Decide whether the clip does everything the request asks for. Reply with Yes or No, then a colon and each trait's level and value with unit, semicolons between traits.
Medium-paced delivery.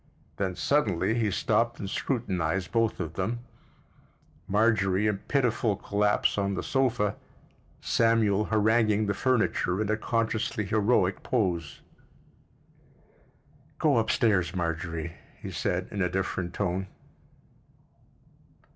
No: slow, 110 wpm